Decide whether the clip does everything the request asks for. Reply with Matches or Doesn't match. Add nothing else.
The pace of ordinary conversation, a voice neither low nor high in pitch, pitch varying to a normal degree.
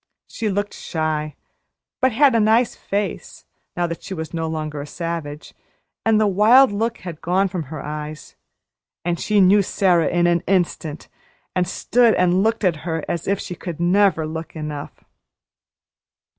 Matches